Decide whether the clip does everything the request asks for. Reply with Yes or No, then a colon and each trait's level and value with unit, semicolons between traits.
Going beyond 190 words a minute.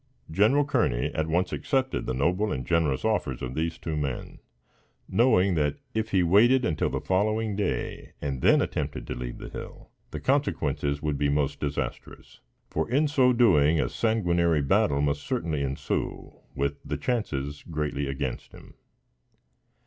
No: average, 155 wpm